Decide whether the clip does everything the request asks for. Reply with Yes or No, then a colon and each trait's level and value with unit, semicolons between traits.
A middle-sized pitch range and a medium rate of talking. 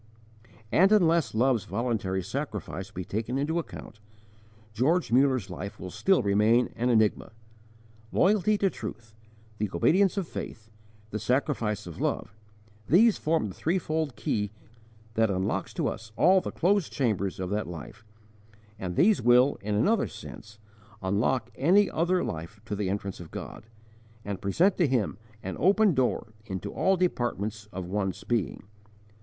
No: wide, 8.1 semitones; average, 150 wpm